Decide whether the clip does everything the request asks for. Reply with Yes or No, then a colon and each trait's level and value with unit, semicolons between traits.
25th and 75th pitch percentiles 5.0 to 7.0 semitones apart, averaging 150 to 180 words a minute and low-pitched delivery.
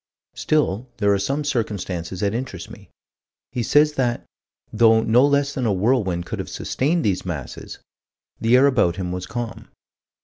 Yes: wide, 5.6 semitones; average, 165 wpm; low, 115 Hz